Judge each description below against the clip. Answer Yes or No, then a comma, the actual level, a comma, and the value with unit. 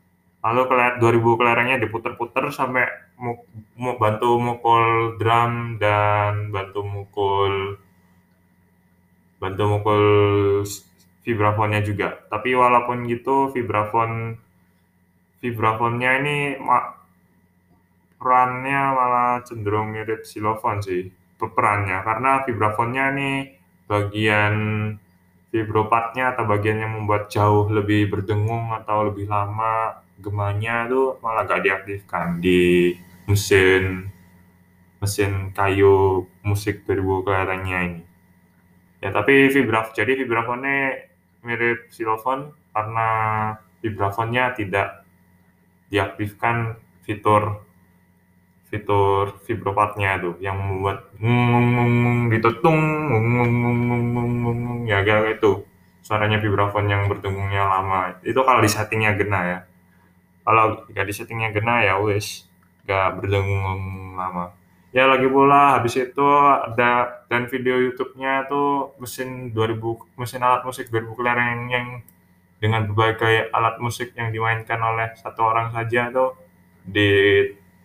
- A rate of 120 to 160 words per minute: No, average, 105 wpm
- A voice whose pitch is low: Yes, low, 105 Hz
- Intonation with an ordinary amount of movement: Yes, average, 3.9 semitones